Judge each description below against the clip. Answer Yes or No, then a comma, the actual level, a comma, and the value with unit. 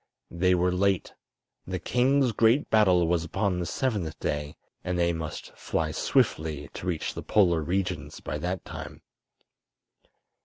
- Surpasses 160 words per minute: No, average, 145 wpm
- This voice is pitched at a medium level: No, very low, 90 Hz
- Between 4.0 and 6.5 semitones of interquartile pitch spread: No, average, 3.6 semitones